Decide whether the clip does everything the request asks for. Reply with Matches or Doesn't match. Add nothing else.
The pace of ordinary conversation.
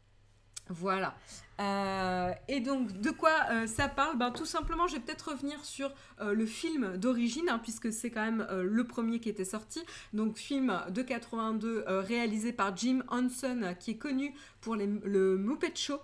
Matches